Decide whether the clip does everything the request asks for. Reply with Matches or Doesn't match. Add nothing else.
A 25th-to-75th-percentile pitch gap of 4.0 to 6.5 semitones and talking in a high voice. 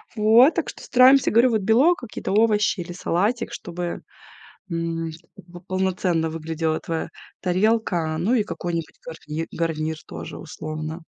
Doesn't match